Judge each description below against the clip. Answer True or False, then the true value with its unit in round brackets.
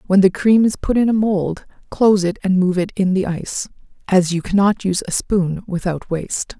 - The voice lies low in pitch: False (190 Hz)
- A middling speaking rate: False (220 wpm)